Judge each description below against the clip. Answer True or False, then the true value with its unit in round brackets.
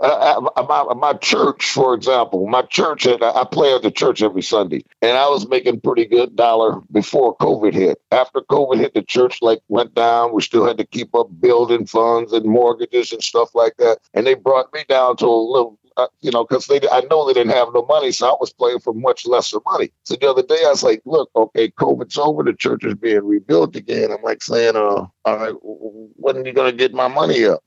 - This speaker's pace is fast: True (230 wpm)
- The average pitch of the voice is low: True (125 Hz)